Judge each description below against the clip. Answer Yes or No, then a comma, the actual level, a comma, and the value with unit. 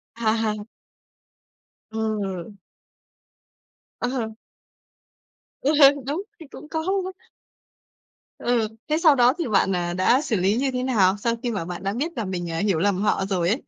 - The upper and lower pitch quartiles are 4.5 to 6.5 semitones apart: Yes, average, 5.2 semitones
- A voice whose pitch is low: No, high, 220 Hz